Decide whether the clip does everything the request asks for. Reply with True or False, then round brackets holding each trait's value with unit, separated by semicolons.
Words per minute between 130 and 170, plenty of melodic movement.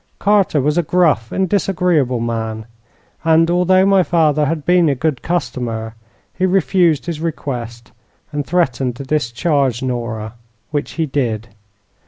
True (140 wpm; 6.2 semitones)